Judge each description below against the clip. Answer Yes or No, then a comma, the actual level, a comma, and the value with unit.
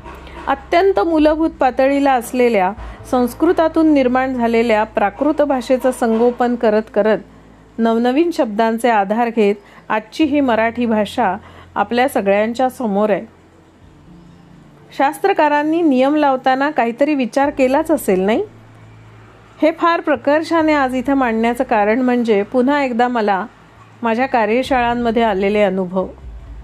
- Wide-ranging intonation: No, average, 4.6 semitones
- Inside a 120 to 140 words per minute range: No, average, 105 wpm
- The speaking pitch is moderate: No, high, 245 Hz